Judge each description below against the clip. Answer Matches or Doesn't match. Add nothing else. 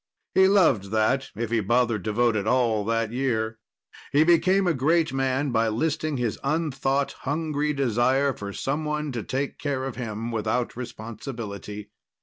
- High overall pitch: Doesn't match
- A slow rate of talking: Doesn't match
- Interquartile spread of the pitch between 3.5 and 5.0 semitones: Matches